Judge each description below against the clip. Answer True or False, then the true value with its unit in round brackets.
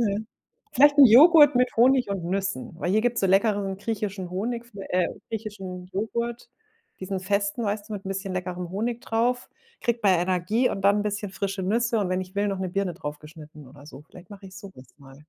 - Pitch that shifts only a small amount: False (3.6 semitones)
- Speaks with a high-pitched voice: True (200 Hz)